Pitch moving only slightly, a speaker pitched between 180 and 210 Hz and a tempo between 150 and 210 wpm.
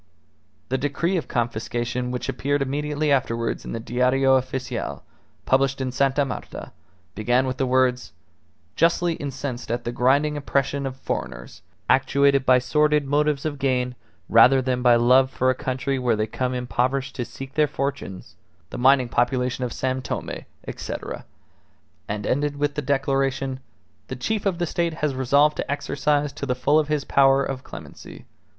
No: narrow, 2.2 semitones; low, 135 Hz; average, 165 wpm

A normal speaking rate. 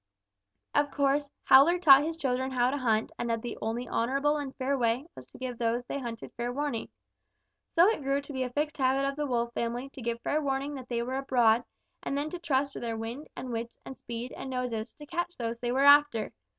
No: fast, 230 wpm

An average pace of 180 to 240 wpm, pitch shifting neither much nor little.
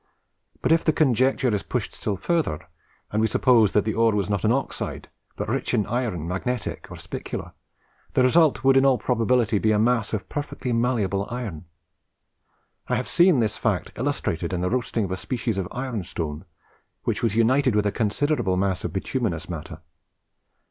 Yes: average, 185 wpm; average, 4.5 semitones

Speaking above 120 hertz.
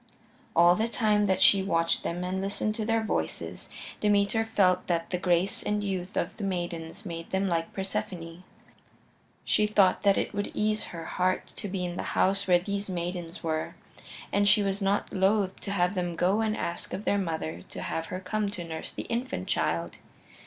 Yes: high, 190 Hz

